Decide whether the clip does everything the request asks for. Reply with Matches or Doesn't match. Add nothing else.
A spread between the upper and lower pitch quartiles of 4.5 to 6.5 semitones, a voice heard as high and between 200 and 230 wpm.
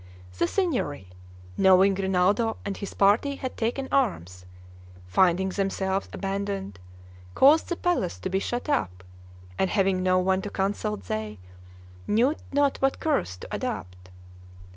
Doesn't match